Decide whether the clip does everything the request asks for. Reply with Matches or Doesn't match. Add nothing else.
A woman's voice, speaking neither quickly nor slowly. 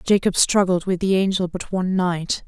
Matches